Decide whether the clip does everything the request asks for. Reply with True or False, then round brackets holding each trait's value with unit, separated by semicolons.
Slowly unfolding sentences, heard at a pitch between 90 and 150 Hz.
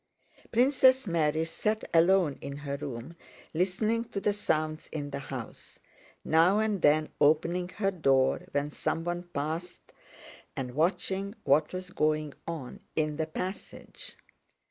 False (130 wpm; 165 Hz)